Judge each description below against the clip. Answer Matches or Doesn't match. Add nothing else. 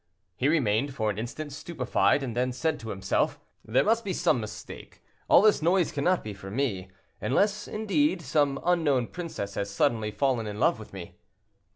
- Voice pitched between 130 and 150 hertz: Matches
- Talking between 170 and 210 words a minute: Matches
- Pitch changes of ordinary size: Doesn't match